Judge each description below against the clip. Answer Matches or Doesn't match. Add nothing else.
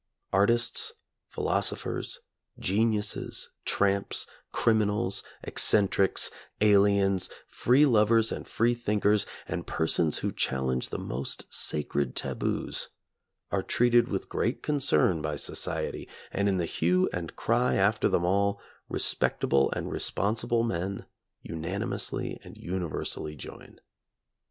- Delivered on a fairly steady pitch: Doesn't match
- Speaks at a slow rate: Matches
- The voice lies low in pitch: Matches